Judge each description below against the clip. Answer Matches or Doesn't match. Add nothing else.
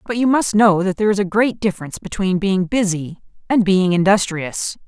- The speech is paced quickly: Doesn't match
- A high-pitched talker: Matches